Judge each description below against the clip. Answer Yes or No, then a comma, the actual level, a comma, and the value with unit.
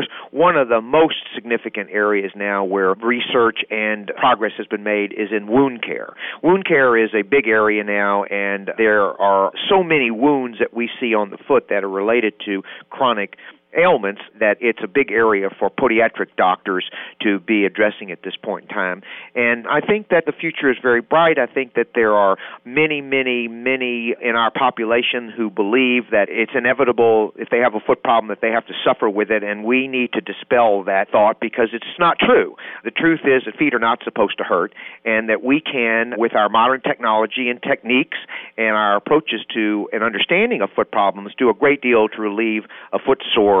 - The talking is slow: No, average, 200 wpm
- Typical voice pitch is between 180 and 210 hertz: No, low, 115 Hz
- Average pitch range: Yes, average, 3.4 semitones